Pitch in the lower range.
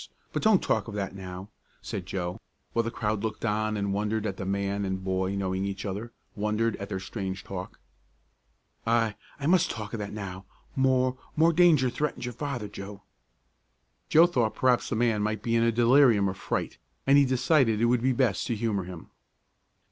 Yes: low, 110 Hz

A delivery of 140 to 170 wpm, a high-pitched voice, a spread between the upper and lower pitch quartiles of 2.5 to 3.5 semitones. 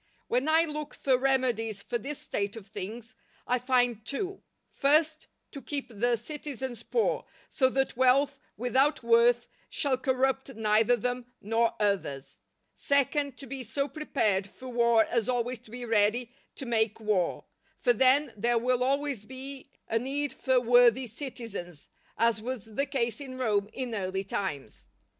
Yes: average, 155 wpm; high, 245 Hz; average, 3.2 semitones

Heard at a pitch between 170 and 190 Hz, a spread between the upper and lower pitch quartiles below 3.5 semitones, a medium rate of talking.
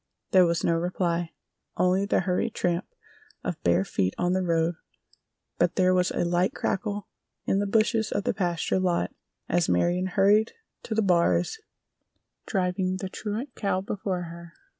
Yes: medium, 185 Hz; narrow, 2.4 semitones; average, 160 wpm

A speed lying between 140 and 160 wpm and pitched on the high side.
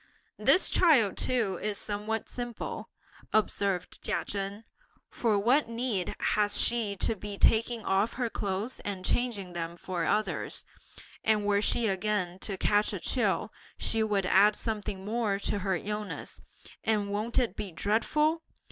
Yes: average, 145 wpm; high, 210 Hz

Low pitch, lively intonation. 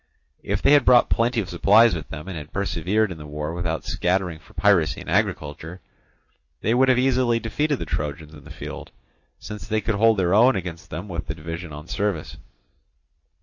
Yes: very low, 95 Hz; wide, 5.8 semitones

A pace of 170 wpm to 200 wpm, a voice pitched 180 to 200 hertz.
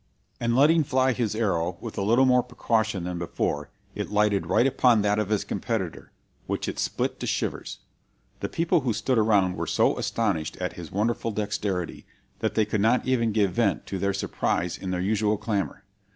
No: average, 190 wpm; low, 105 Hz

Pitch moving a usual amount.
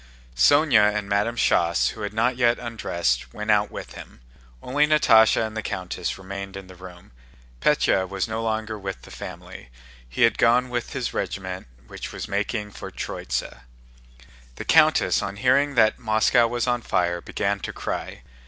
Yes: average, 3.4 semitones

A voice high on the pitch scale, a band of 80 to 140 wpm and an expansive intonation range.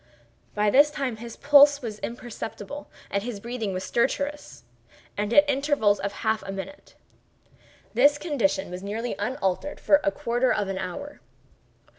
No: high, 235 Hz; average, 150 wpm; wide, 6.0 semitones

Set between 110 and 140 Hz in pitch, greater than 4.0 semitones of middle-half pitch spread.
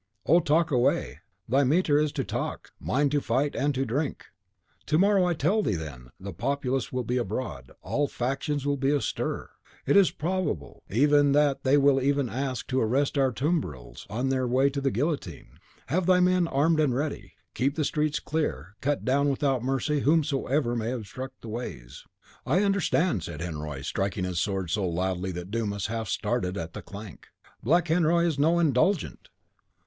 Yes: low, 135 Hz; wide, 5.6 semitones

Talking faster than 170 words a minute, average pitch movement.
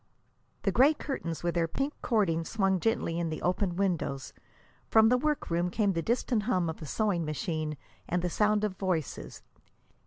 Yes: average, 180 wpm; average, 4.6 semitones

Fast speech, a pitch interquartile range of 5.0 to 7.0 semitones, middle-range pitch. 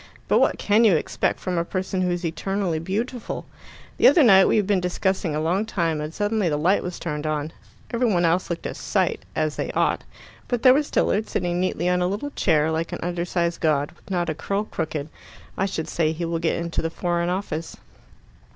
No: fast, 215 wpm; average, 3.2 semitones; medium, 175 Hz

